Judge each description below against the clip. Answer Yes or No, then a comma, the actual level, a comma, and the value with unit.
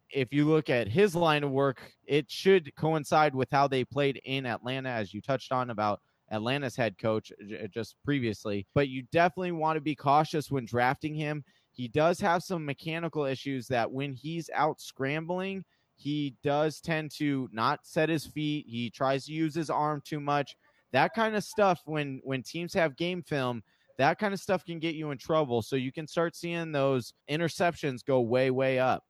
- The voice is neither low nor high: Yes, medium, 145 Hz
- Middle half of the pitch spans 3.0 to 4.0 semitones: Yes, average, 3.6 semitones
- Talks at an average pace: Yes, average, 195 wpm